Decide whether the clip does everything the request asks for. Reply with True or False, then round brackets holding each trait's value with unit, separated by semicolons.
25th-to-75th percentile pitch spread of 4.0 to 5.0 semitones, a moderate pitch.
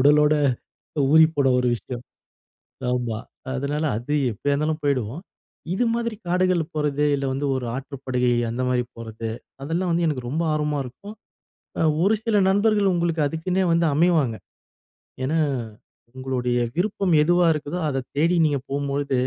True (4.7 semitones; 150 Hz)